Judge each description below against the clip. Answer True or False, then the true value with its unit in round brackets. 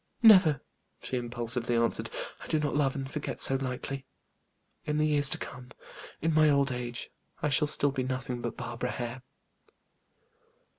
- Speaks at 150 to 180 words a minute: True (160 wpm)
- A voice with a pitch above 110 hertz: True (135 Hz)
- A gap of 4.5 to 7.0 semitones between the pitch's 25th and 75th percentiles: False (3.2 semitones)